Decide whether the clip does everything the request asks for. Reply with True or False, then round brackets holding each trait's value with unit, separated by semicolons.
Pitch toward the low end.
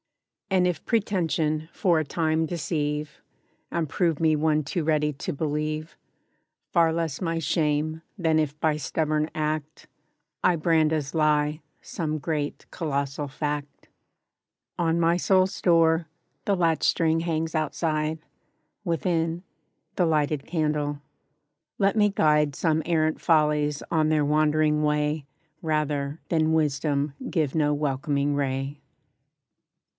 False (155 Hz)